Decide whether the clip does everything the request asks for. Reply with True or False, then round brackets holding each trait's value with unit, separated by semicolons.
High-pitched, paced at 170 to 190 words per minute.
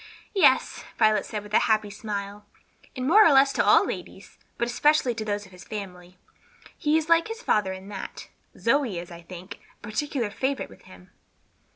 True (215 Hz; 185 wpm)